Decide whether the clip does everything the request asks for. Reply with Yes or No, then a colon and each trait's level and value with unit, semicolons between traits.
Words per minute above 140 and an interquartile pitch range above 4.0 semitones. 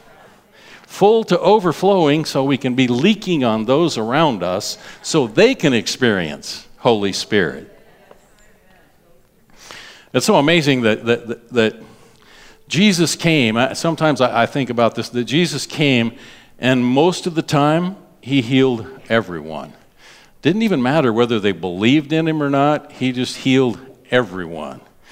No: slow, 135 wpm; average, 5.2 semitones